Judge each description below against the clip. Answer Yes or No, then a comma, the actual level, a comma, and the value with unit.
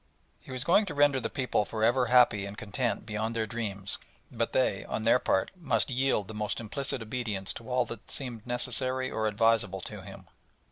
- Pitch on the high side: No, low, 115 Hz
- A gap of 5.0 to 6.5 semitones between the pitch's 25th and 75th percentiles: No, average, 3.2 semitones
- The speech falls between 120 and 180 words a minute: No, average, 195 wpm